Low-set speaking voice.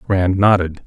Yes: very low, 95 Hz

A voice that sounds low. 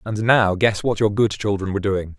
Yes: low, 100 Hz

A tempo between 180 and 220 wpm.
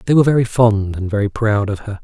No: fast, 265 wpm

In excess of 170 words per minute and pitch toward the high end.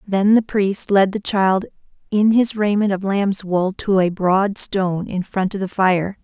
Yes: average, 200 wpm; high, 195 Hz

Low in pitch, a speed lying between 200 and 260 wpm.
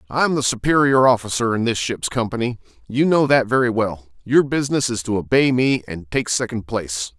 No: low, 115 Hz; average, 175 wpm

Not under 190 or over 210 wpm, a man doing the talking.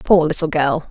No: average, 200 wpm; female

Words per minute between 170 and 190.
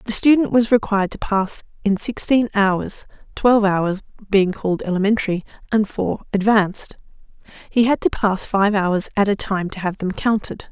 No: average, 160 wpm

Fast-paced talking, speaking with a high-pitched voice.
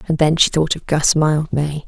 No: fast, 225 wpm; medium, 155 Hz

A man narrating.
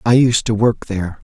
Yes: male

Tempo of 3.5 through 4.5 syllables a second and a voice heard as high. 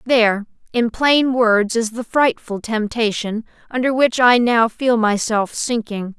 Yes: 4.0 syllables/s; high, 230 Hz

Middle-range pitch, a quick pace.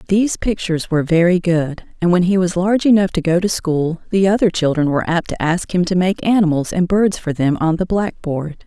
Yes: medium, 175 Hz; fast, 230 wpm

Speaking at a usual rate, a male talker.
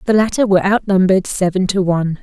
No: average, 190 wpm; female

